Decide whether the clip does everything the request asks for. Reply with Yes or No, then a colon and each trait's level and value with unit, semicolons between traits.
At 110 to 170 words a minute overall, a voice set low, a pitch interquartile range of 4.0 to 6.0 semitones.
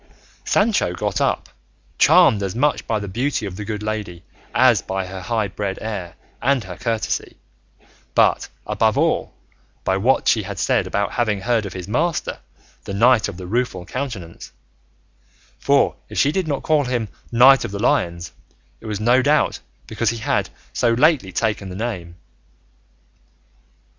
Yes: average, 165 wpm; low, 110 Hz; average, 4.5 semitones